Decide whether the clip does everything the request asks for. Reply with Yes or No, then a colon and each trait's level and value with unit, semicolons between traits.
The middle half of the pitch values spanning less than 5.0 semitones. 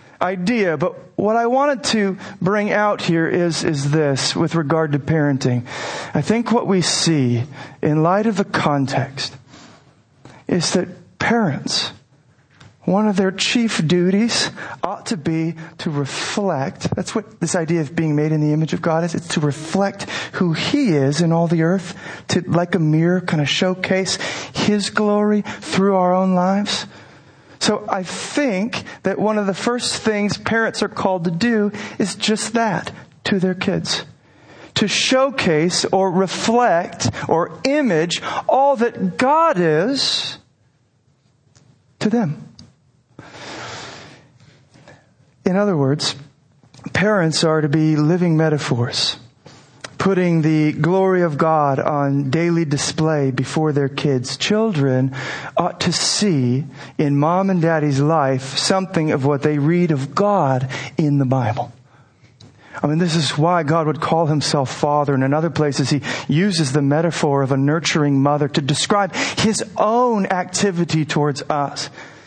No: average, 5.3 semitones